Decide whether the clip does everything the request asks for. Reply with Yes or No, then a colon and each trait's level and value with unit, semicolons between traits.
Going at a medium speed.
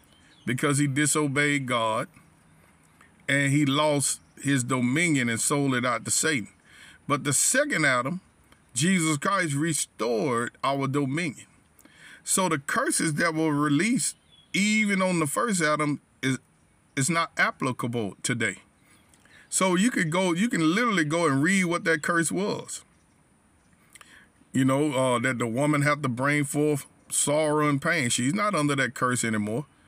Yes: average, 145 wpm